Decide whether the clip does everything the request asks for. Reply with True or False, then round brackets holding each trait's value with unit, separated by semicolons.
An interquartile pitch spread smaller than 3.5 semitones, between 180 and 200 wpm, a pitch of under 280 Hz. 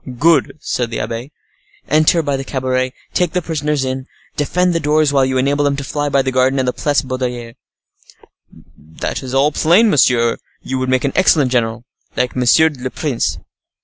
True (2.8 semitones; 185 wpm; 135 Hz)